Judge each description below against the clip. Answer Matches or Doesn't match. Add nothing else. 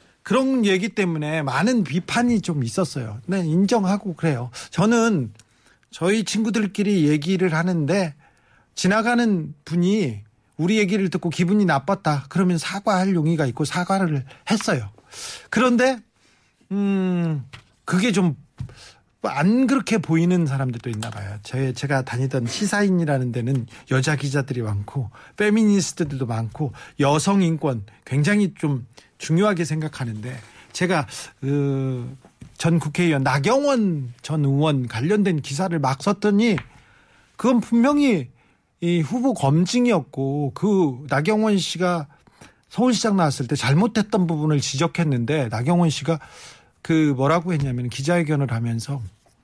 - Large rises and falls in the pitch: Matches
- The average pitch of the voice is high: Doesn't match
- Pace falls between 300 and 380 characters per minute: Doesn't match